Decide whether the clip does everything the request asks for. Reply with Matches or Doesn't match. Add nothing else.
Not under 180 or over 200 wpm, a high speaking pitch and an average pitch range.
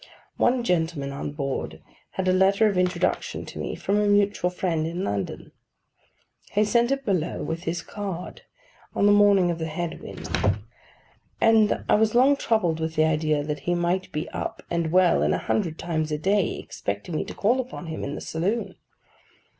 Doesn't match